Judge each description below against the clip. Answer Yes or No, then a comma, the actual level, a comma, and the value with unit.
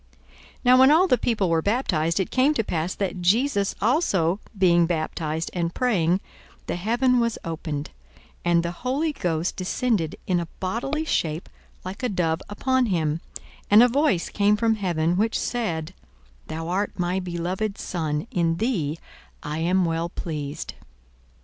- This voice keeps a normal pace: Yes, average, 160 wpm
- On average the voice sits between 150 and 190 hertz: Yes, medium, 185 Hz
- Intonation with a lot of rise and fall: Yes, wide, 5.7 semitones